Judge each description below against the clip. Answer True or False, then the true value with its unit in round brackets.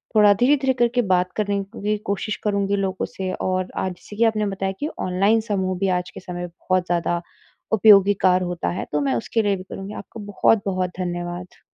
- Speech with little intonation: True (2.3 semitones)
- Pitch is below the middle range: False (195 Hz)